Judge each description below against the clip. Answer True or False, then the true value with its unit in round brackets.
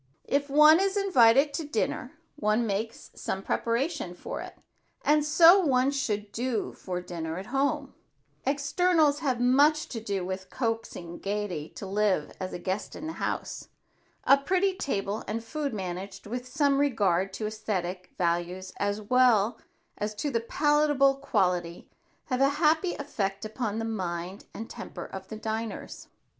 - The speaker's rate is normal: True (155 wpm)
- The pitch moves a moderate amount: False (6.5 semitones)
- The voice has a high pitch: True (225 Hz)